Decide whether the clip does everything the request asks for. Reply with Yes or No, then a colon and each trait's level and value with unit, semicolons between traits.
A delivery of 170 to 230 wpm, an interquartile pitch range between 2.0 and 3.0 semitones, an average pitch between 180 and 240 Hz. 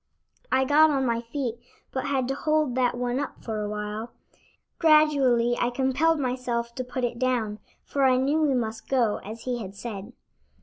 No: average, 180 wpm; narrow, 2.6 semitones; very high, 250 Hz